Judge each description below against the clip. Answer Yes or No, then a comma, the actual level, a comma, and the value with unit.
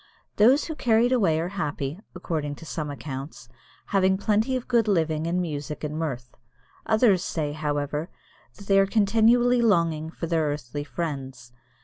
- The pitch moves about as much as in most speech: No, wide, 5.9 semitones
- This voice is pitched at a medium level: Yes, medium, 165 Hz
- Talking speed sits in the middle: Yes, average, 160 wpm